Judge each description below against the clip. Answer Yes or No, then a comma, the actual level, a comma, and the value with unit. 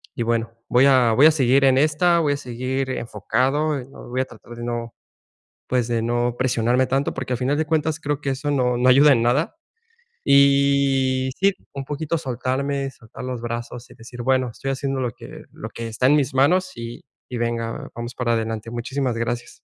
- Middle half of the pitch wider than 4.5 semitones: No, average, 2.8 semitones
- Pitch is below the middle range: Yes, low, 130 Hz